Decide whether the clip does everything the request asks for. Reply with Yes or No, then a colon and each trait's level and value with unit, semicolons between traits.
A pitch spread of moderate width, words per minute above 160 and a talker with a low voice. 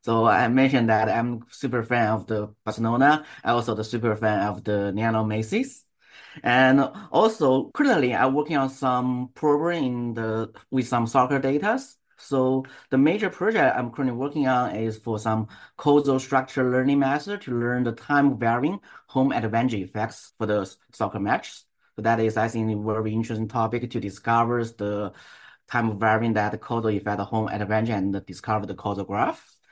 Yes: average, 3.2 semitones; average, 170 wpm; low, 115 Hz